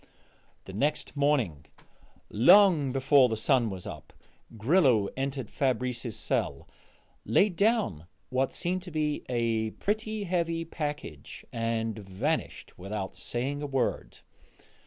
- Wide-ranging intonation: Yes, wide, 6.1 semitones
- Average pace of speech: No, slow, 115 wpm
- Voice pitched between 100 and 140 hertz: Yes, low, 135 Hz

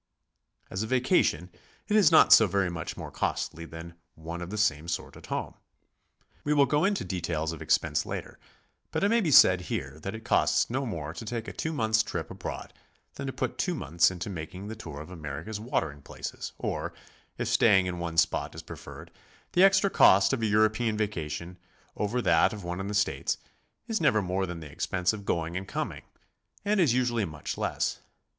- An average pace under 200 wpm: No, fast, 205 wpm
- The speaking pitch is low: Yes, very low, 95 Hz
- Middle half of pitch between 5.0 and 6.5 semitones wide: Yes, wide, 5.6 semitones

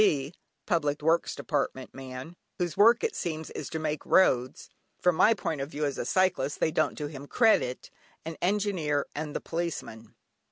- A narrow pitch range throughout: No, average, 3.8 semitones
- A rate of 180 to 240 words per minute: No, average, 170 wpm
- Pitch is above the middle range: No, medium, 155 Hz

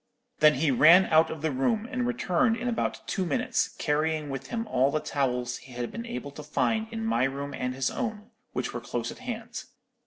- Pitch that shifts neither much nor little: No, wide, 8.8 semitones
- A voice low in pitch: No, medium, 155 Hz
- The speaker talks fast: Yes, fast, 215 wpm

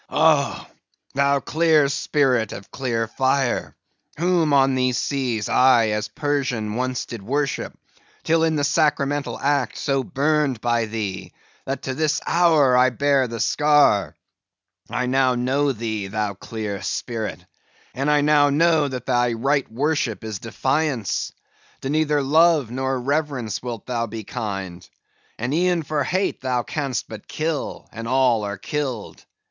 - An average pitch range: Yes, average, 4.2 semitones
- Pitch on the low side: Yes, low, 130 Hz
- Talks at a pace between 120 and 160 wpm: Yes, average, 145 wpm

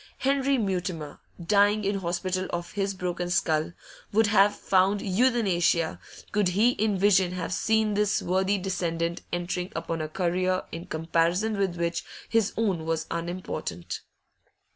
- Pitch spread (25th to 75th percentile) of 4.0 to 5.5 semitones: No, average, 3.1 semitones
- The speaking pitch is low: No, medium, 185 Hz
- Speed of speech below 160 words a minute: Yes, average, 140 wpm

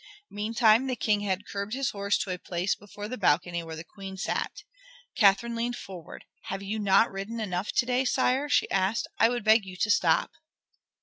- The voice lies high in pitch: Yes, high, 205 Hz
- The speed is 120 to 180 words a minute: No, average, 195 wpm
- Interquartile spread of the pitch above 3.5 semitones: No, average, 3.2 semitones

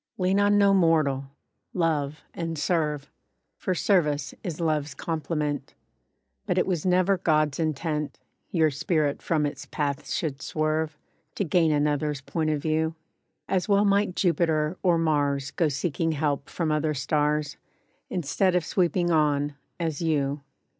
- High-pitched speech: No, medium, 155 Hz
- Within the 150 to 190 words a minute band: No, average, 140 wpm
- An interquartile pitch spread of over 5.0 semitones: No, average, 2.7 semitones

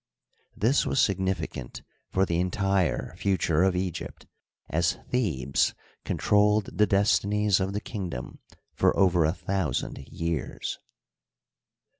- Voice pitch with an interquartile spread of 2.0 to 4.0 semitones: Yes, average, 3.3 semitones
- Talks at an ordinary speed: No, slow, 115 wpm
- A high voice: No, very low, 95 Hz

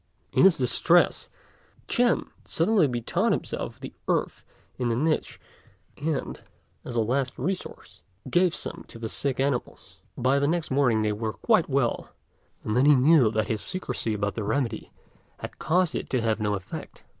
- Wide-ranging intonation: Yes, wide, 6.1 semitones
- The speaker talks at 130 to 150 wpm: No, average, 170 wpm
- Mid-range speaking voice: No, low, 130 Hz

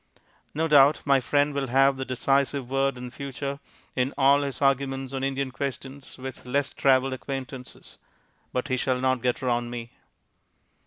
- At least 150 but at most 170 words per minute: Yes, average, 160 wpm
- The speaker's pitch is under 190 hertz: Yes, low, 135 Hz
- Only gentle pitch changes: Yes, narrow, 1.3 semitones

